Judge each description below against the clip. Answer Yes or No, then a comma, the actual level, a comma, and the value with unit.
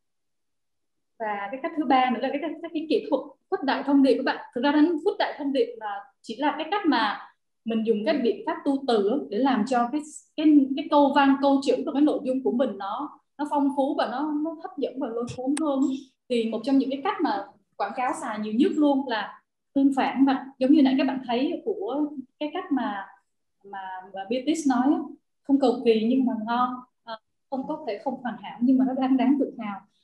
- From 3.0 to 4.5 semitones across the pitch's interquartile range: Yes, average, 3.6 semitones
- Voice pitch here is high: Yes, very high, 270 Hz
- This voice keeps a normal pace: Yes, average, 230 wpm